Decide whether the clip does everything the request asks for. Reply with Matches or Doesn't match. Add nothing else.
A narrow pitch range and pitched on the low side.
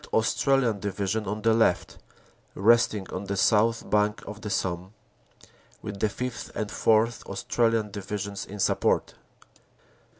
Matches